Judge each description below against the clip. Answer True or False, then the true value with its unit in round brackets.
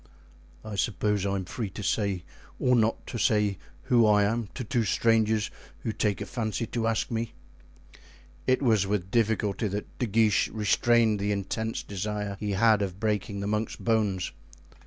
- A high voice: False (105 Hz)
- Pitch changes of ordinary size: False (2.0 semitones)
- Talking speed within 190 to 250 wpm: False (170 wpm)